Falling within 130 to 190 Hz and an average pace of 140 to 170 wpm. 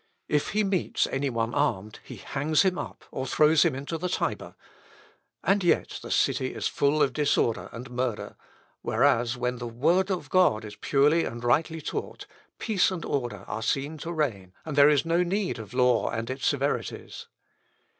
No: medium, 140 Hz; average, 180 wpm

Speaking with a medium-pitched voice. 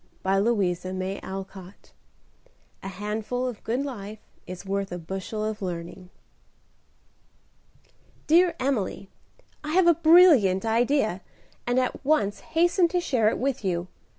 No: high, 215 Hz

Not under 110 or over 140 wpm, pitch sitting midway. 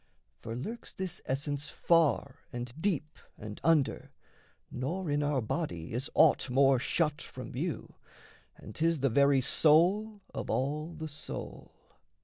Yes: slow, 135 wpm; medium, 145 Hz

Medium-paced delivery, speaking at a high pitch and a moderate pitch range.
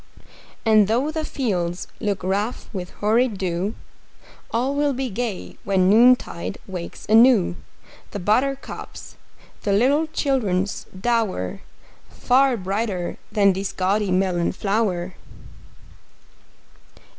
No: slow, 105 wpm; high, 210 Hz; average, 4.7 semitones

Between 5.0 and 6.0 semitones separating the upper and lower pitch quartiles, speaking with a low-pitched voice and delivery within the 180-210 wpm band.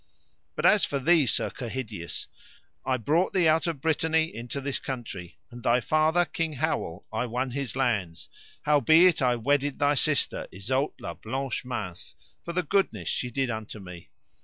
No: wide, 5.4 semitones; low, 130 Hz; average, 165 wpm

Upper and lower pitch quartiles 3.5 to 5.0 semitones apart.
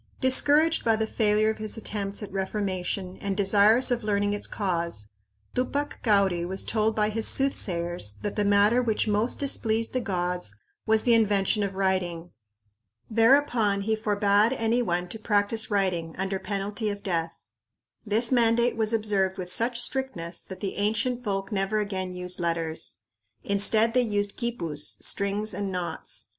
No: average, 2.9 semitones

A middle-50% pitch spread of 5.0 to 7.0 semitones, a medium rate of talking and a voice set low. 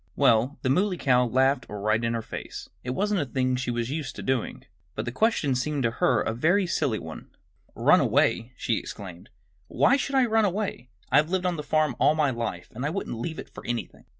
No: wide, 5.6 semitones; fast, 220 wpm; low, 130 Hz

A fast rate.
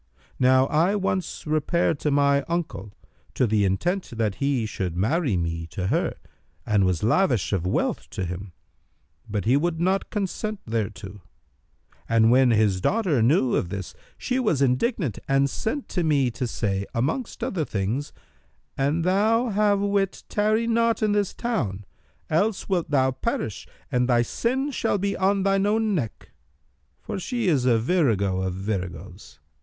No: average, 160 wpm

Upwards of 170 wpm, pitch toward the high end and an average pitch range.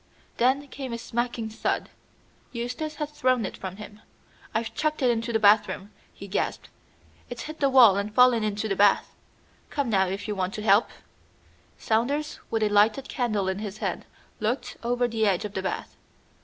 Yes: average, 185 wpm; high, 225 Hz; average, 3.3 semitones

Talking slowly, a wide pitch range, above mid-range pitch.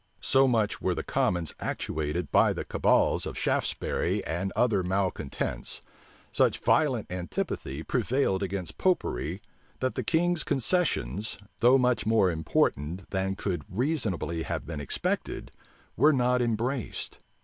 No: slow, 125 wpm; wide, 6.3 semitones; low, 100 Hz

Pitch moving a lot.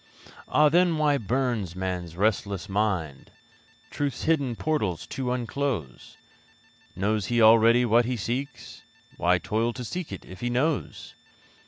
Yes: wide, 5.7 semitones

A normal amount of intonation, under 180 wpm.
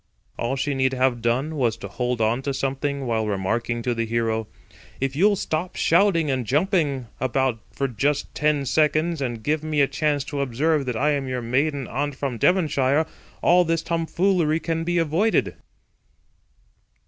Yes: average, 4.1 semitones; average, 170 wpm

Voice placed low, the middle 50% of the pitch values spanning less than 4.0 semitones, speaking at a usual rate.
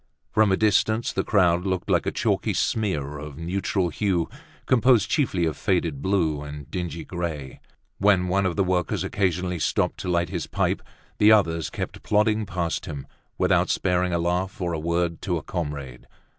Yes: very low, 90 Hz; average, 3.0 semitones; average, 175 wpm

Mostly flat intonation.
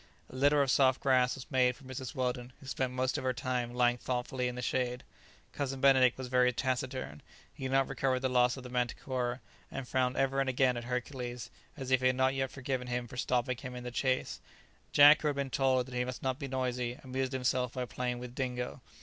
Yes: narrow, 1.1 semitones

